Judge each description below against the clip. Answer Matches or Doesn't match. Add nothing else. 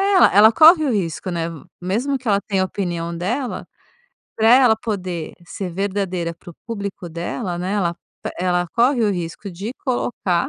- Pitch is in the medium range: Doesn't match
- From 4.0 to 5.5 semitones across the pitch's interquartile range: Matches